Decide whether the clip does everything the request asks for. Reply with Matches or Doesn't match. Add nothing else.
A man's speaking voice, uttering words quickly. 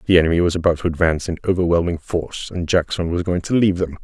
Matches